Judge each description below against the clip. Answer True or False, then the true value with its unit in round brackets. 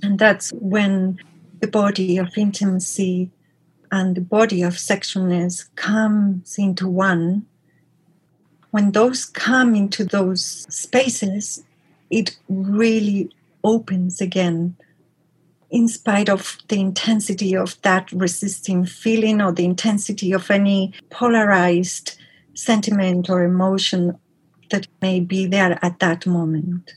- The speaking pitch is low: False (190 Hz)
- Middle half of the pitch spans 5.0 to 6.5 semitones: False (2.6 semitones)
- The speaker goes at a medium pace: False (110 wpm)